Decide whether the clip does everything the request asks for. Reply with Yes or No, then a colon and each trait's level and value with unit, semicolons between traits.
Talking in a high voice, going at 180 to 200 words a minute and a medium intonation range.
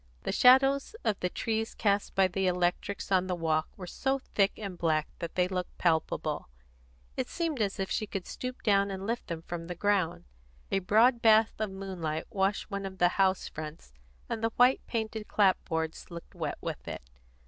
Yes: high, 195 Hz; average, 190 wpm; average, 3.8 semitones